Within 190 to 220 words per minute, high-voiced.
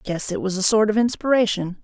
No: fast, 230 wpm; high, 205 Hz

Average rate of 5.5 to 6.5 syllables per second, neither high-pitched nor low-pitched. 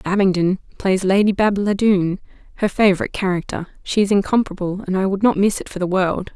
No: 6.0 syllables/s; high, 195 Hz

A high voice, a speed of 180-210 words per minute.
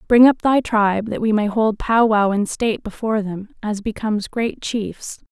Yes: high, 215 Hz; fast, 205 wpm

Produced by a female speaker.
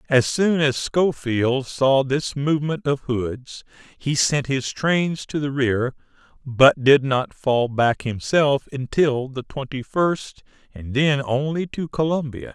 No: male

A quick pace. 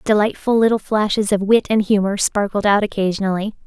No: average, 165 wpm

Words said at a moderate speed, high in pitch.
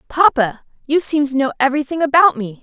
Yes: average, 185 wpm; very high, 280 Hz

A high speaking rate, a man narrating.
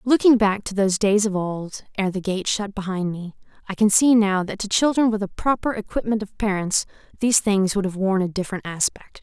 No: fast, 220 wpm; female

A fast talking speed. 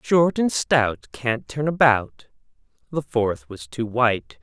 No: average, 150 wpm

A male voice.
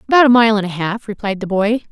No: female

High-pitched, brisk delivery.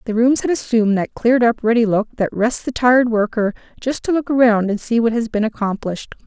Yes: high, 230 Hz; fast, 230 wpm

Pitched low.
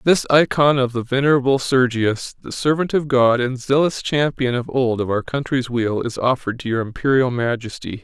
Yes: low, 130 Hz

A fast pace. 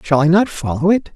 Yes: fast, 260 wpm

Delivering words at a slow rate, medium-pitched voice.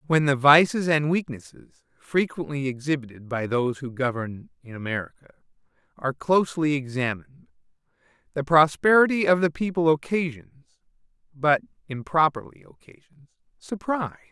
Yes: slow, 100 wpm; medium, 150 Hz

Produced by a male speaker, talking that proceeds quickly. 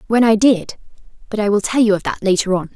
No: female; fast, 240 wpm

